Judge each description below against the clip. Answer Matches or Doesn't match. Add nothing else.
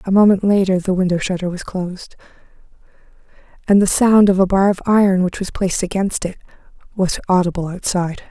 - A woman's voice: Matches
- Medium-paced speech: Matches